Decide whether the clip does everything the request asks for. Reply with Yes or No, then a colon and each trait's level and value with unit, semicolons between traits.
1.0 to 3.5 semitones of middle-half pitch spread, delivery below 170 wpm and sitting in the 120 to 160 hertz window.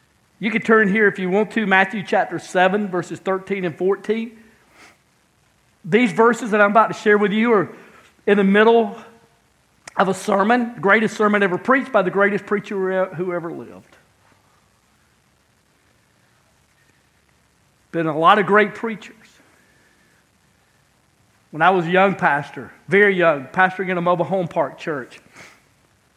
No: average, 2.9 semitones; average, 145 wpm; high, 200 Hz